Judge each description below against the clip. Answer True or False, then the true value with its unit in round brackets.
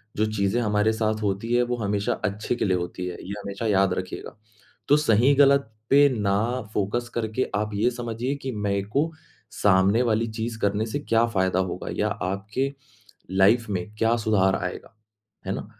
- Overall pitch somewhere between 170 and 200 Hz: False (105 Hz)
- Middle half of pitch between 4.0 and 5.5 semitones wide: False (3.2 semitones)